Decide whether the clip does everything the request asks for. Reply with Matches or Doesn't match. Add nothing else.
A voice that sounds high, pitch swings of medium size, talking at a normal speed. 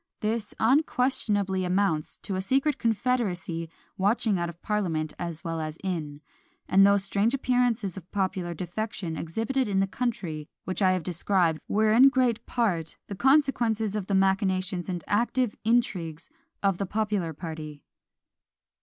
Matches